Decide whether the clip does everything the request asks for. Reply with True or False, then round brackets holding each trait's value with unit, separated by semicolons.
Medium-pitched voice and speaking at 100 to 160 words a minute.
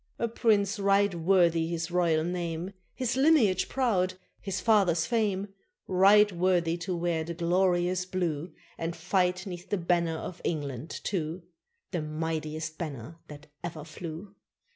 True (175 Hz; 140 wpm)